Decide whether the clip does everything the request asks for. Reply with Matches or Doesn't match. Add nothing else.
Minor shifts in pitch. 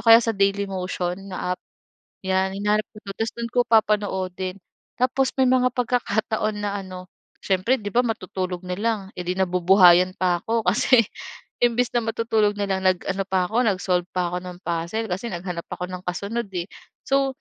Doesn't match